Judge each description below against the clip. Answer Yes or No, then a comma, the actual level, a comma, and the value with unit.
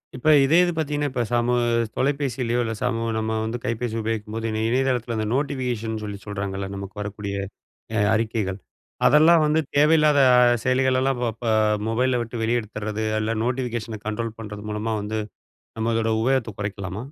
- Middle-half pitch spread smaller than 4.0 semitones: Yes, average, 3.1 semitones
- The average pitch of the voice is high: No, low, 115 Hz